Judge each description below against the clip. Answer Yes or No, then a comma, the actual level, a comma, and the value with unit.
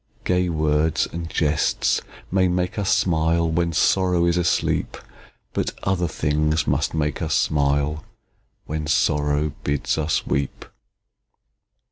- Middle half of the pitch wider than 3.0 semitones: No, narrow, 2.5 semitones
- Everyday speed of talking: No, slow, 120 wpm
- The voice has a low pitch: Yes, very low, 80 Hz